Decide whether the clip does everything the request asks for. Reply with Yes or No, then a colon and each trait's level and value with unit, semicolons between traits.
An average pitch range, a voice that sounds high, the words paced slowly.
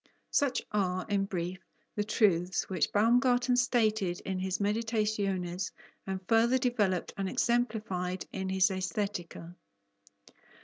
Yes: average, 3.4 semitones; high, 200 Hz; slow, 115 wpm